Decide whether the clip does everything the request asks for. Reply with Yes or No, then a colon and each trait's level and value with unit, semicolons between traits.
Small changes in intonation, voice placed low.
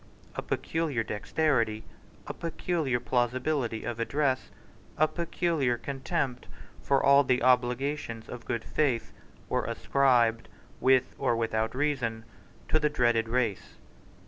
No: average, 3.7 semitones; low, 125 Hz